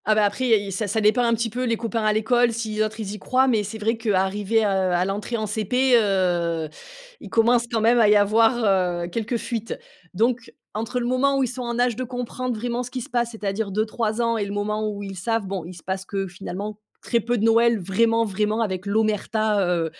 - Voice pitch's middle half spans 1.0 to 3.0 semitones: Yes, average, 2.7 semitones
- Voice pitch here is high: Yes, high, 220 Hz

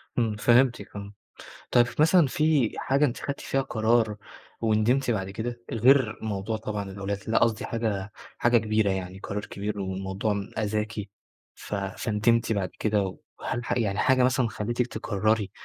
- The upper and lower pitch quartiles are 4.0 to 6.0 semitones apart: No, average, 2.9 semitones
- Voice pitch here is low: Yes, low, 110 Hz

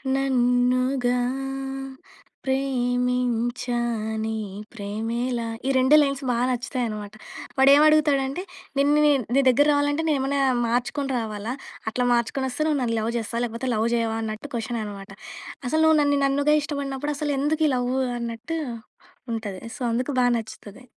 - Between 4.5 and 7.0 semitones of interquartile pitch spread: No, average, 3.3 semitones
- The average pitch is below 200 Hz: No, very high, 250 Hz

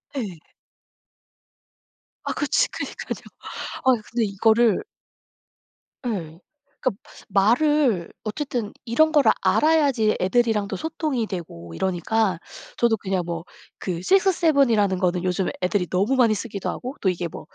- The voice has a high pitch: Yes, high, 215 Hz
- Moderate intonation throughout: No, wide, 5.7 semitones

